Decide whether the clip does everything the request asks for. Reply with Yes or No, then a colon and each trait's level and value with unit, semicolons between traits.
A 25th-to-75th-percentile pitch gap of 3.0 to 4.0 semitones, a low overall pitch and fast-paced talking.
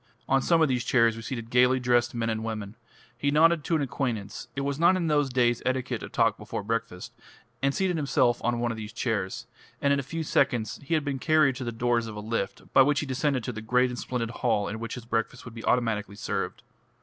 Yes: average, 3.4 semitones; low, 125 Hz; fast, 245 wpm